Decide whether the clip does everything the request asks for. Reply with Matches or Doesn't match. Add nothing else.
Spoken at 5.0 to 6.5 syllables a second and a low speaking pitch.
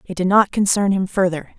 Doesn't match